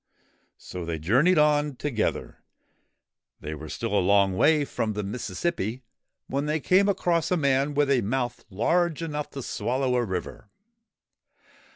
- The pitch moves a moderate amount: No, wide, 6.5 semitones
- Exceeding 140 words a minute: Yes, average, 150 wpm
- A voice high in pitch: No, low, 130 Hz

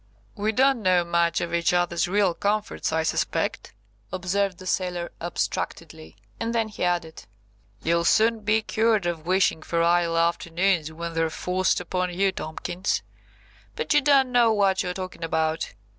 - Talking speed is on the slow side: No, average, 160 wpm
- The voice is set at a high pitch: No, medium, 180 Hz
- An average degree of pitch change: Yes, average, 3.5 semitones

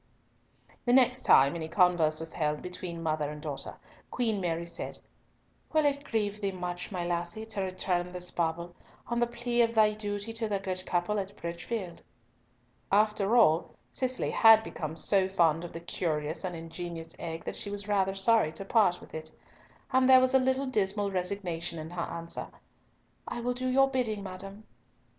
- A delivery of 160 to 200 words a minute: Yes, average, 180 wpm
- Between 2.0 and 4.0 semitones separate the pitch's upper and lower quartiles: No, average, 4.6 semitones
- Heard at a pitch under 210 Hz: Yes, high, 190 Hz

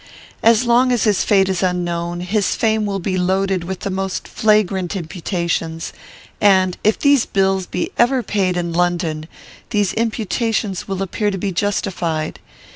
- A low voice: No, high, 190 Hz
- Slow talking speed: No, average, 155 wpm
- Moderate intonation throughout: Yes, average, 3.1 semitones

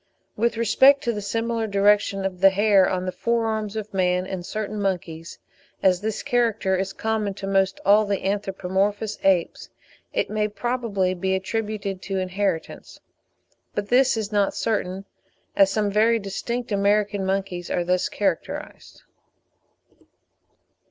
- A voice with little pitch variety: Yes, narrow, 2.3 semitones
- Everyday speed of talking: Yes, average, 145 wpm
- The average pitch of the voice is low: No, high, 200 Hz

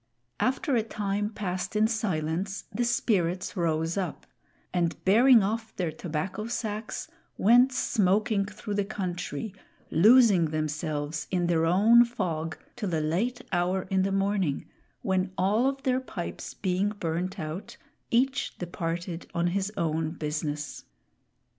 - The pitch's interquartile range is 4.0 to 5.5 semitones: Yes, average, 4.6 semitones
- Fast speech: No, slow, 135 wpm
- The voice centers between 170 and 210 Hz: Yes, high, 190 Hz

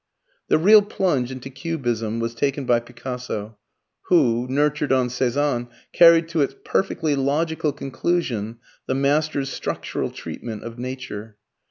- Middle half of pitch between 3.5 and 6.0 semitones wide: Yes, average, 3.9 semitones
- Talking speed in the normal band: No, slow, 130 wpm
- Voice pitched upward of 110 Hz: Yes, low, 135 Hz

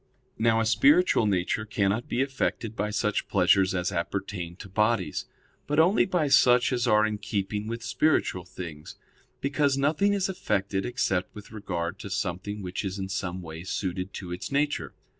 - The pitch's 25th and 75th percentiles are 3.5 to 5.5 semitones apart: Yes, average, 4.8 semitones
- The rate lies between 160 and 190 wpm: Yes, average, 170 wpm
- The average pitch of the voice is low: Yes, low, 105 Hz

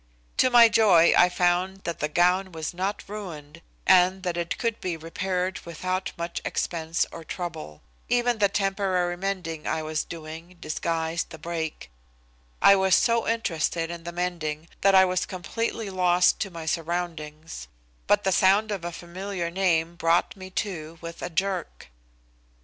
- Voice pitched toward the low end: No, medium, 175 Hz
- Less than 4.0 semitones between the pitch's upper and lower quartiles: Yes, narrow, 2.6 semitones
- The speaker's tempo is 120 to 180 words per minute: Yes, average, 160 wpm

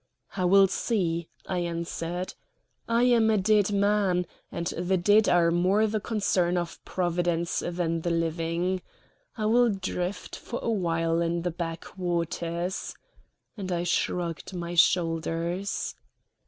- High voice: No, medium, 175 Hz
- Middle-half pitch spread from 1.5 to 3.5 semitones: Yes, average, 2.7 semitones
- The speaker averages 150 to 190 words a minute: No, slow, 135 wpm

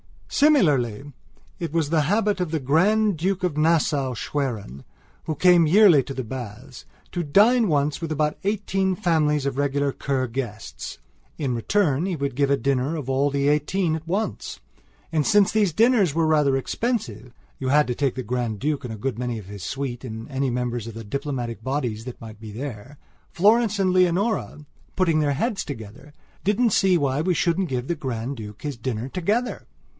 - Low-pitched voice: No, medium, 145 Hz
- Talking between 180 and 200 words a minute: Yes, average, 185 wpm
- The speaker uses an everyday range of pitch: No, wide, 6.0 semitones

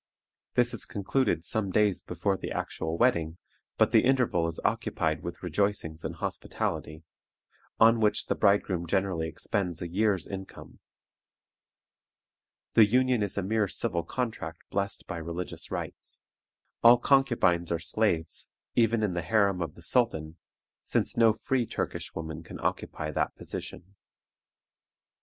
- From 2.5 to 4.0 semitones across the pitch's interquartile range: No, average, 4.9 semitones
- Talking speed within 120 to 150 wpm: Yes, average, 140 wpm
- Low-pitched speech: Yes, very low, 95 Hz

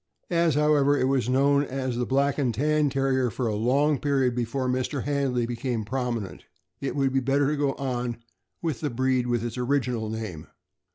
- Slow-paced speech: No, average, 185 wpm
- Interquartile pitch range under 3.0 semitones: Yes, narrow, 2.6 semitones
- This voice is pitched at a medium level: No, low, 130 Hz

